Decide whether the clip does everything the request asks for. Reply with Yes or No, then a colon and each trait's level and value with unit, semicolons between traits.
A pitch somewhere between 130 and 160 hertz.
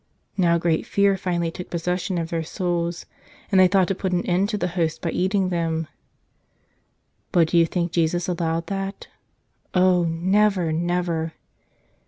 No: medium, 175 Hz